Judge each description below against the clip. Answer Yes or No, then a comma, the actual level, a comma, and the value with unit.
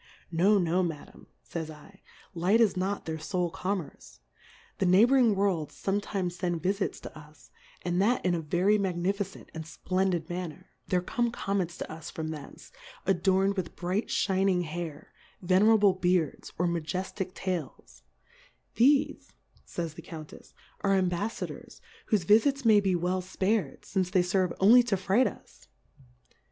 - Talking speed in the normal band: Yes, average, 150 wpm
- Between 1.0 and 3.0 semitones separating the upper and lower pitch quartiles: Yes, narrow, 2.6 semitones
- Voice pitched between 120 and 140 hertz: No, medium, 185 Hz